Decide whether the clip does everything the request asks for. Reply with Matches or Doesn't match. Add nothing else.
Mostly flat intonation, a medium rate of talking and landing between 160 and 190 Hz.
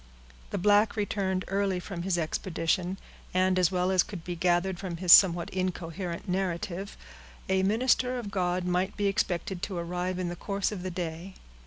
Matches